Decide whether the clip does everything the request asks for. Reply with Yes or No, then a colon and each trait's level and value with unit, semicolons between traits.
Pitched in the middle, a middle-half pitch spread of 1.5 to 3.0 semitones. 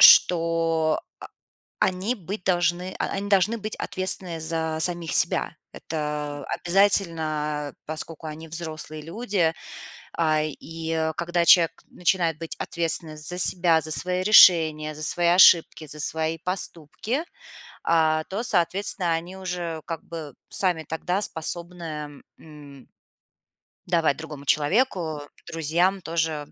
Yes: medium, 165 Hz; narrow, 2.4 semitones